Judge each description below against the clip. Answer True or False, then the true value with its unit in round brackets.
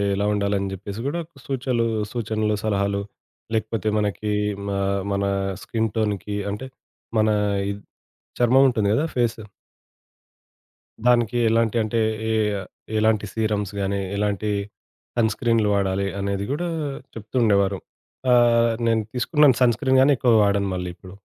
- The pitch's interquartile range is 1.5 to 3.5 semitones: True (2.9 semitones)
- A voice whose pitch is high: False (110 Hz)